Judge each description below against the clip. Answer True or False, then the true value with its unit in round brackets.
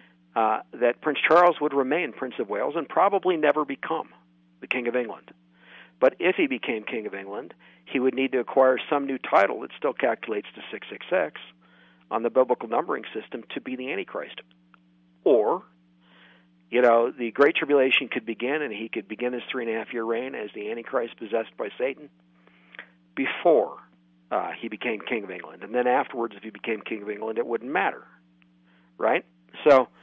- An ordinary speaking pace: True (185 wpm)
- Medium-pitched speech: False (115 Hz)